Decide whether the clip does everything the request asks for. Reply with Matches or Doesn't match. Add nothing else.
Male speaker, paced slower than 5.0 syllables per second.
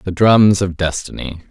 Matches